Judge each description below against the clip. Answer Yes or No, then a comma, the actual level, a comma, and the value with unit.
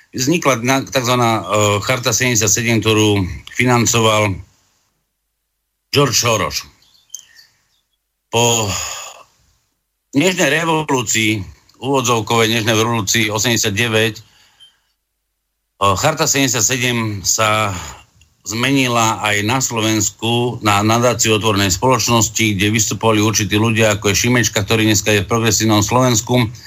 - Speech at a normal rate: No, slow, 90 wpm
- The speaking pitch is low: Yes, low, 110 Hz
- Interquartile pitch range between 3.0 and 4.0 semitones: No, narrow, 2.6 semitones